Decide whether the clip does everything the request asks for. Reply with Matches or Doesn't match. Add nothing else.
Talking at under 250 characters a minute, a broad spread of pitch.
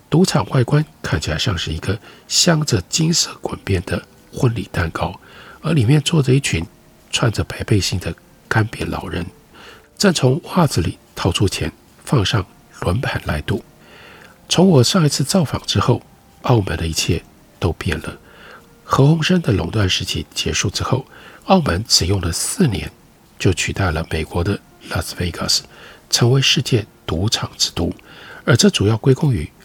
Matches